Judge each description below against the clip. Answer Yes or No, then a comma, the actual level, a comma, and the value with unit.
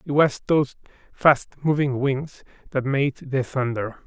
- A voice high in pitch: No, low, 135 Hz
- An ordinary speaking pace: Yes, average, 150 wpm